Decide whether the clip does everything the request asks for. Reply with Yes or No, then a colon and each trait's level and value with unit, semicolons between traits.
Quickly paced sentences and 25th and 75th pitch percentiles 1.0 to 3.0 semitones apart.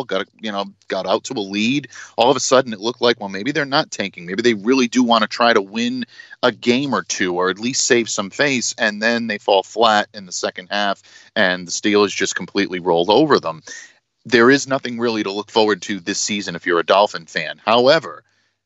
No: fast, 235 wpm; average, 4.1 semitones